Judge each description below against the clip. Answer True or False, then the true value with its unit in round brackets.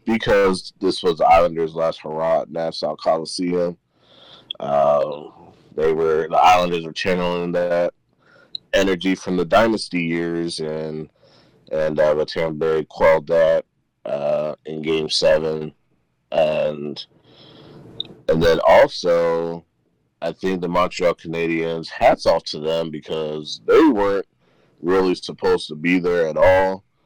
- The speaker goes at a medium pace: False (125 wpm)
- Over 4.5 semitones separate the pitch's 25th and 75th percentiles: False (3.2 semitones)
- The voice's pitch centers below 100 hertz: True (85 Hz)